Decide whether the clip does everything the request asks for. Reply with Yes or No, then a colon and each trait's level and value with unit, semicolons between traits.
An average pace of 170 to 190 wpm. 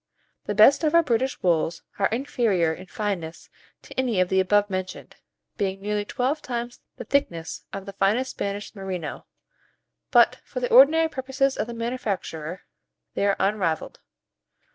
No: average, 155 wpm